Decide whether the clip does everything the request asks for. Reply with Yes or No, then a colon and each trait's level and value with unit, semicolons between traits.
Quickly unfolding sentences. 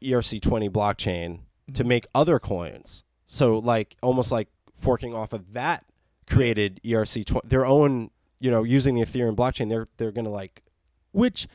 No: average, 160 wpm